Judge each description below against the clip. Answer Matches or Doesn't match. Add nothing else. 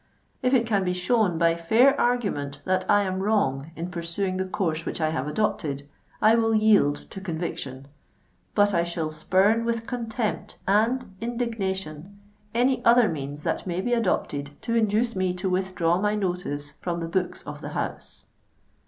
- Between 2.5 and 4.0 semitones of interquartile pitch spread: Doesn't match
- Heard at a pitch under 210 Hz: Matches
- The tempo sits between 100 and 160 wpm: Doesn't match